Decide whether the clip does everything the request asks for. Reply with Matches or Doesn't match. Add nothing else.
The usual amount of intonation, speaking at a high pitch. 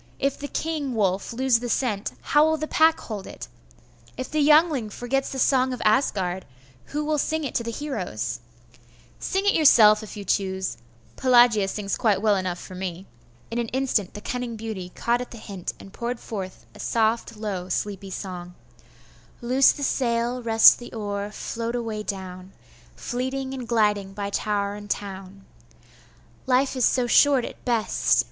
Matches